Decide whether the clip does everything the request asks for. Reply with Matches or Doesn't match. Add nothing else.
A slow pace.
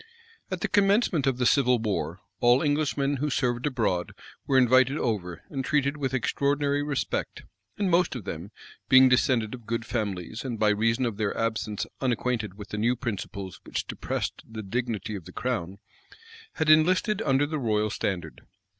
Doesn't match